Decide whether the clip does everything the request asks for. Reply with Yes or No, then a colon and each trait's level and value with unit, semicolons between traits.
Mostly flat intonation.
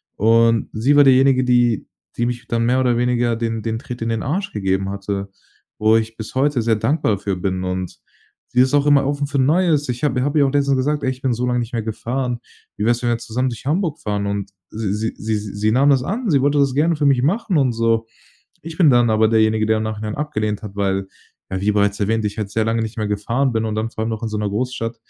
No: average, 3.7 semitones